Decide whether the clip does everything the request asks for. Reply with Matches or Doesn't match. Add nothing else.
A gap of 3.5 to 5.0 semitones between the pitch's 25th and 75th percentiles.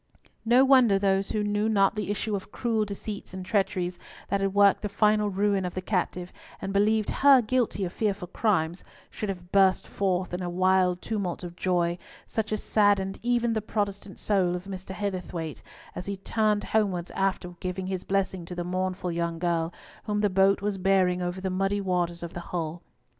Doesn't match